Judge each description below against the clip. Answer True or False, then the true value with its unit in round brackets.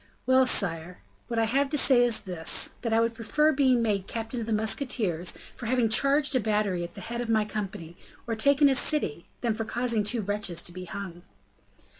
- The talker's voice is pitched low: False (225 Hz)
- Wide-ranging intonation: False (4.1 semitones)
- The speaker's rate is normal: False (210 wpm)